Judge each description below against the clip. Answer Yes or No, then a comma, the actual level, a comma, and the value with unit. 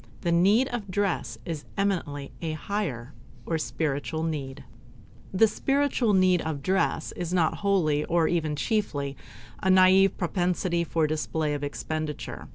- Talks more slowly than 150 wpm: Yes, average, 140 wpm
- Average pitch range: Yes, average, 4.0 semitones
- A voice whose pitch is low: No, medium, 170 Hz